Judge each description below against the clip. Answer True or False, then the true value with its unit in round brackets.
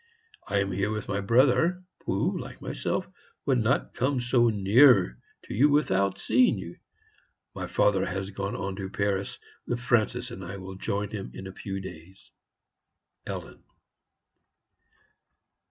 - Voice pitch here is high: False (100 Hz)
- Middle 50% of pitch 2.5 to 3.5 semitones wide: False (4.1 semitones)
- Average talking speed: True (145 wpm)